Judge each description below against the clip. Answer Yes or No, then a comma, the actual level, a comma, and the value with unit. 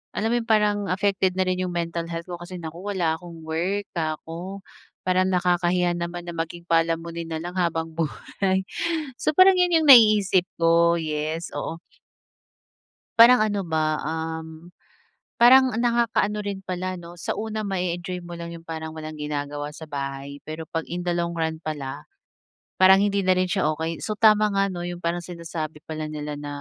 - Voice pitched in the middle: Yes, medium, 175 Hz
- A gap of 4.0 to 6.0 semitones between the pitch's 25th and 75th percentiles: No, average, 3.0 semitones